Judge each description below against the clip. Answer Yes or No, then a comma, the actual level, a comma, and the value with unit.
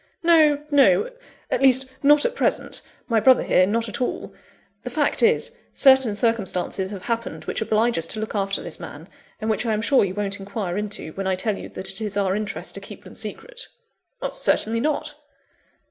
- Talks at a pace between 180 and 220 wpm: Yes, average, 195 wpm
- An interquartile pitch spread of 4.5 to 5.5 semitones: Yes, average, 5.2 semitones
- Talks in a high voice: Yes, high, 220 Hz